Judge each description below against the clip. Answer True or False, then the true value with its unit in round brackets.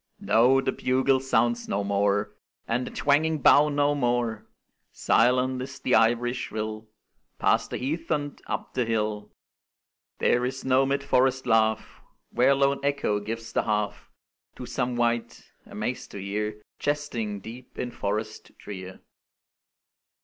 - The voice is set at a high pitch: False (120 Hz)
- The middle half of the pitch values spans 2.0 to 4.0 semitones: True (3.7 semitones)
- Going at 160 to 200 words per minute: False (140 wpm)